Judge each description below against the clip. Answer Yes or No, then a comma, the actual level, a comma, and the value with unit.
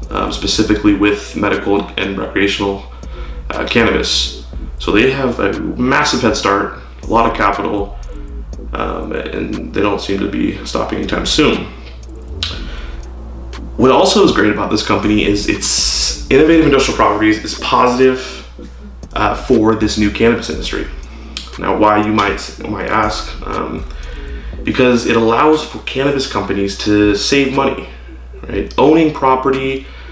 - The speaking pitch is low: Yes, very low, 90 Hz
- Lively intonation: Yes, wide, 8.8 semitones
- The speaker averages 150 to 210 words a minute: No, slow, 135 wpm